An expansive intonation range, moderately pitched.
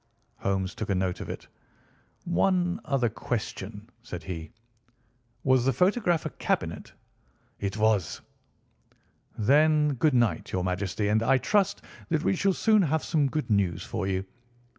No: wide, 8.3 semitones; low, 120 Hz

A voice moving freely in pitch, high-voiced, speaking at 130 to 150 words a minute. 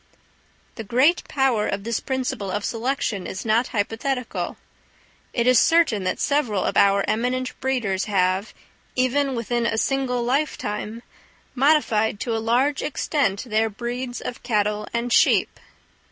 No: average, 3.7 semitones; high, 235 Hz; average, 140 wpm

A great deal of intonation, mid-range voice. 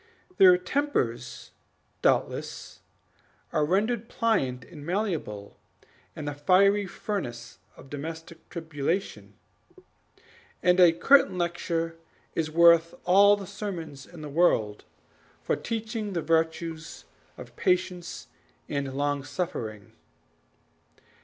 No: average, 4.5 semitones; medium, 165 Hz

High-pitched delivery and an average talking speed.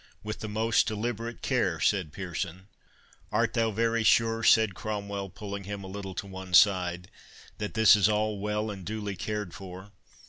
No: low, 105 Hz; average, 170 wpm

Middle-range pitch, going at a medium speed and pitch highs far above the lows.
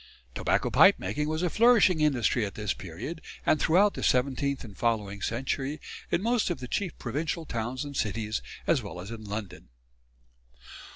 No: low, 130 Hz; average, 170 wpm; wide, 6.6 semitones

